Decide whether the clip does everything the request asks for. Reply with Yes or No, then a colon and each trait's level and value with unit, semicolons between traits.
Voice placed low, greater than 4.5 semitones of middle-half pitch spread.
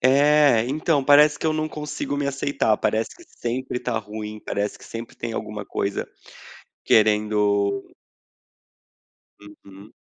Yes: low, 115 Hz; wide, 5.4 semitones